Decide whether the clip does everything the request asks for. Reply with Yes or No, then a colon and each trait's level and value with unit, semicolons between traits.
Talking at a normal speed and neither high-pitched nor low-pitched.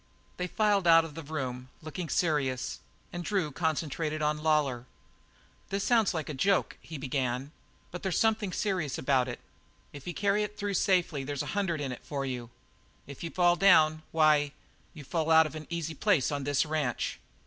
Yes: average, 185 wpm; medium, 155 Hz